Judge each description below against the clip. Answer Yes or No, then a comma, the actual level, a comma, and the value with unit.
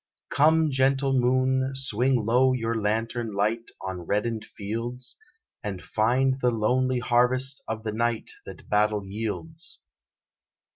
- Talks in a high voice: No, low, 120 Hz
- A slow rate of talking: Yes, slow, 125 wpm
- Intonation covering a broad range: No, average, 3.2 semitones